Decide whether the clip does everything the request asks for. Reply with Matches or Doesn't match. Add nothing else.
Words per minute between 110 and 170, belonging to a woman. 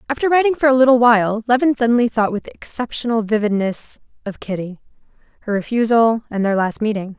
Matches